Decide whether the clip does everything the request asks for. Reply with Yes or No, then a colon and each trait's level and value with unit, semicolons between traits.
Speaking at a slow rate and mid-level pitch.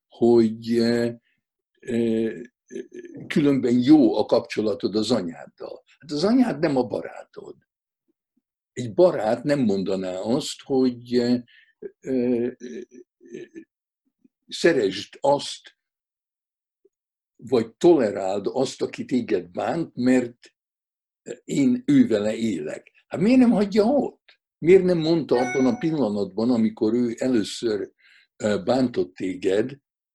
Yes: slow, 95 wpm; medium, 175 Hz